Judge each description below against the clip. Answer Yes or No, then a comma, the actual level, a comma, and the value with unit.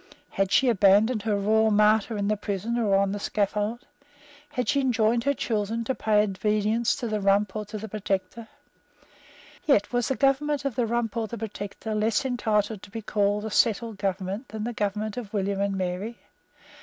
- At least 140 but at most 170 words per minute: No, average, 195 wpm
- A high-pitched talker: Yes, high, 215 Hz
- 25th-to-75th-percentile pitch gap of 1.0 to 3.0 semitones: Yes, narrow, 2.4 semitones